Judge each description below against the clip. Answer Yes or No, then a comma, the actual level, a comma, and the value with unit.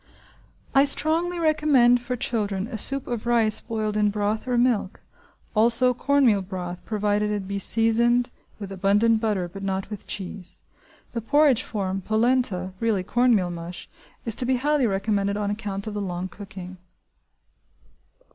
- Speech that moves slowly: No, average, 145 wpm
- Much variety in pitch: No, average, 3.6 semitones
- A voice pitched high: Yes, high, 215 Hz